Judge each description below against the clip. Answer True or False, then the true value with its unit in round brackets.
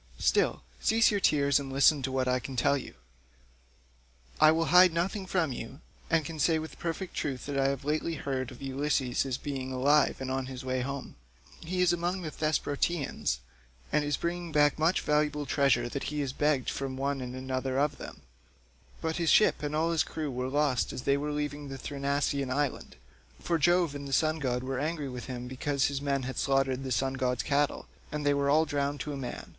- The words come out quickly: True (210 wpm)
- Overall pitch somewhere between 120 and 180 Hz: True (140 Hz)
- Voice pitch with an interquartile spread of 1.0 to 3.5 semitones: True (2.7 semitones)